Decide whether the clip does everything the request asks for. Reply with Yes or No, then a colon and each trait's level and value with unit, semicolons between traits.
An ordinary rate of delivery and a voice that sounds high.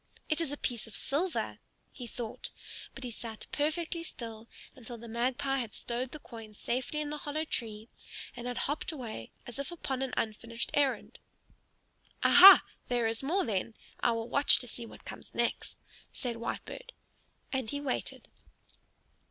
Yes: average, 165 wpm; very high, 250 Hz